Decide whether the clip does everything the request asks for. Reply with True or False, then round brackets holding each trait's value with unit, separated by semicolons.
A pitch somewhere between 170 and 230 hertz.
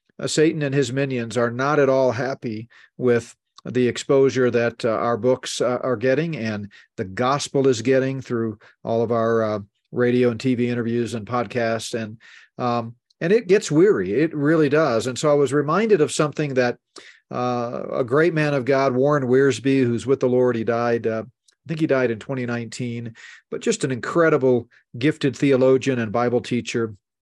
False (125 Hz)